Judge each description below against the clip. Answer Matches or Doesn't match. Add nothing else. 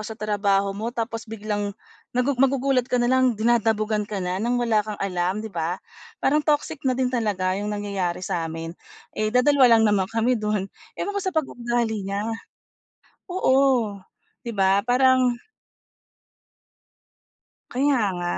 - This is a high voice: Matches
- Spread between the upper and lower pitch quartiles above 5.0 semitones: Doesn't match